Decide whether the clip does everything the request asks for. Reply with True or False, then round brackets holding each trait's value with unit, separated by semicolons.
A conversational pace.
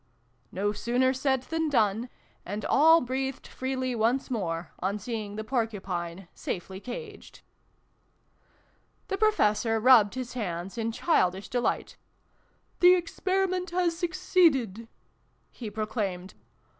False (120 wpm)